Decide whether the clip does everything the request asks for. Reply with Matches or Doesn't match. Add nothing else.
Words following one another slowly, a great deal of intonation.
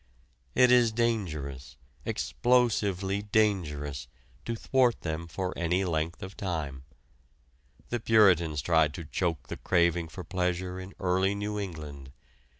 Doesn't match